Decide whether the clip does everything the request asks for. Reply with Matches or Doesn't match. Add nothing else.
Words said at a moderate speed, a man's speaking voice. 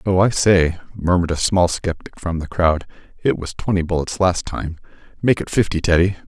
Matches